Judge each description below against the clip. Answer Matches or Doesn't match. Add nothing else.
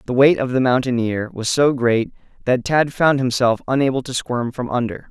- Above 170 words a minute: Matches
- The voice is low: Matches